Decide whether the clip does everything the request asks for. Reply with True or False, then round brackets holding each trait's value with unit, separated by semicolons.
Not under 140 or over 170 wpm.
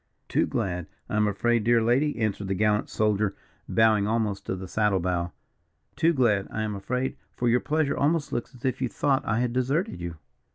False (200 wpm)